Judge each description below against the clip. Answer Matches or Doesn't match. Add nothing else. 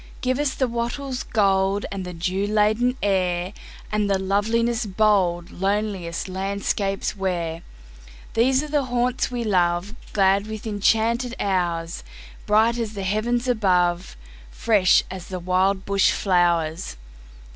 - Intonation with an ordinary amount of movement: Matches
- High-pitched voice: Matches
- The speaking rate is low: Matches